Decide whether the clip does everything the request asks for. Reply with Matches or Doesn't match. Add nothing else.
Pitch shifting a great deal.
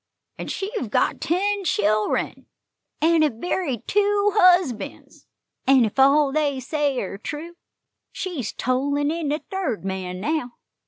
Matches